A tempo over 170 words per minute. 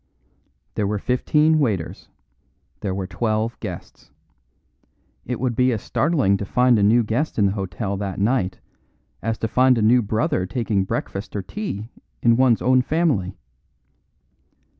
No: average, 150 wpm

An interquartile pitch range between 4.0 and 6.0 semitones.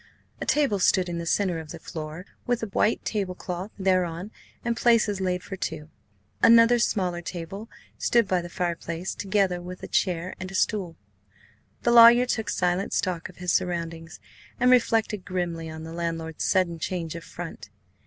No: average, 3.5 semitones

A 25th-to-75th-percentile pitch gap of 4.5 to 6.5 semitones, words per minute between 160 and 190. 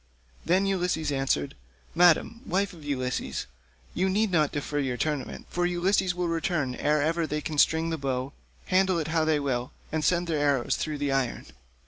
No: average, 3.8 semitones; average, 180 wpm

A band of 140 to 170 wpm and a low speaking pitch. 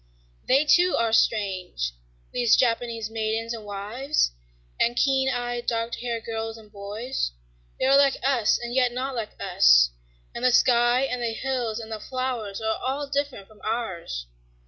No: average, 165 wpm; high, 235 Hz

